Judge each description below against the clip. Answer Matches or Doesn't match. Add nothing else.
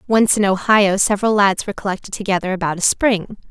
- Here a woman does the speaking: Matches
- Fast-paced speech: Doesn't match